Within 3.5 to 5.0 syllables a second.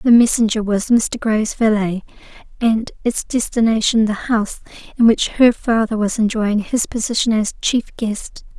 Yes: 4.5 syllables/s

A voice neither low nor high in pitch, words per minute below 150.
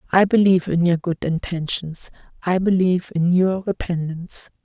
Yes: medium, 175 Hz; average, 140 wpm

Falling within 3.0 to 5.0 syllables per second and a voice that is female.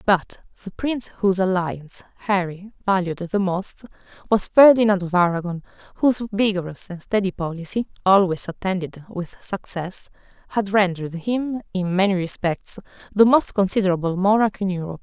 No: 5.3 syllables/s; female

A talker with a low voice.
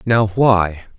Yes: low, 105 Hz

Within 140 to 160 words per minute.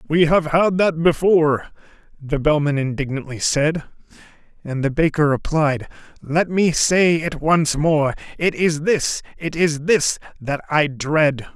Yes: average, 145 wpm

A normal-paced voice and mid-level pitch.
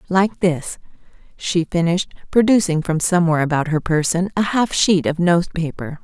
Yes: average, 160 wpm; medium, 170 Hz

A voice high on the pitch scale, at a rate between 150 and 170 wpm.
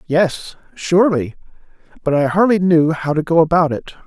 No: medium, 165 Hz; average, 160 wpm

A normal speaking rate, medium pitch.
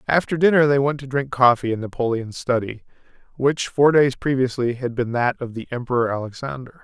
No: average, 185 wpm; low, 130 Hz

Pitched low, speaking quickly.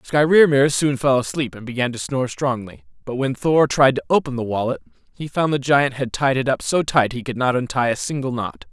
Yes: low, 130 Hz; fast, 235 wpm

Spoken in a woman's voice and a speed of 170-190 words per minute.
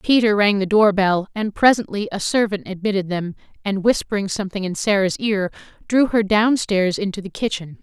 Yes: female; average, 175 wpm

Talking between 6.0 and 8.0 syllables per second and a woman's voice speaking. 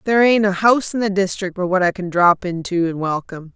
Yes: 6.1 syllables/s; female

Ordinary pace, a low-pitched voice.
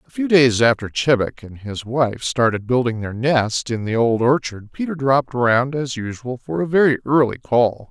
Yes: average, 195 wpm; low, 125 Hz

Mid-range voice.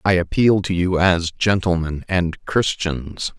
No: very low, 90 Hz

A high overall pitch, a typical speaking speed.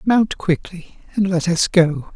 No: medium, 180 Hz; average, 165 wpm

